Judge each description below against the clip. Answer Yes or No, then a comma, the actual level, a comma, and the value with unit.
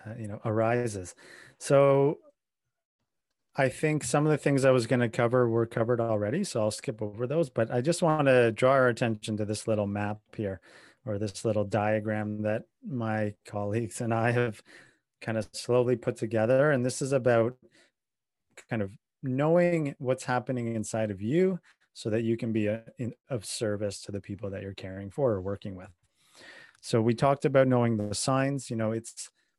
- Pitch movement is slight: No, average, 3.6 semitones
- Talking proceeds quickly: No, average, 190 wpm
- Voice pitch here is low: Yes, low, 115 Hz